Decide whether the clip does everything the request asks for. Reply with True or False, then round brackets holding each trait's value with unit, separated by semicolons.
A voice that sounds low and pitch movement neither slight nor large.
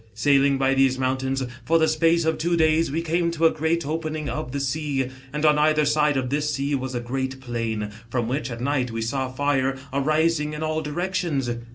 False (145 Hz; 3.1 semitones)